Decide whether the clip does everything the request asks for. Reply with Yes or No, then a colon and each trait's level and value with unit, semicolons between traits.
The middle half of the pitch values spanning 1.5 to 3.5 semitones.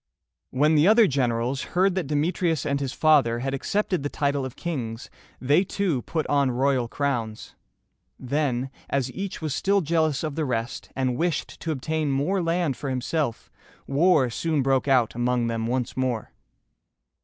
No: average, 4.1 semitones